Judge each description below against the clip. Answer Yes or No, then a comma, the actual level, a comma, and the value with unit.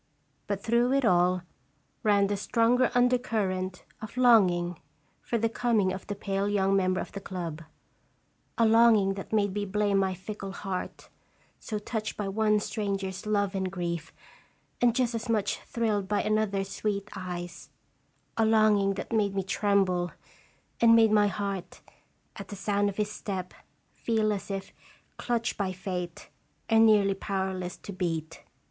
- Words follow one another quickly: No, average, 155 wpm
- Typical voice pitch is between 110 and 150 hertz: No, high, 200 Hz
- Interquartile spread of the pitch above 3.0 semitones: No, narrow, 2.4 semitones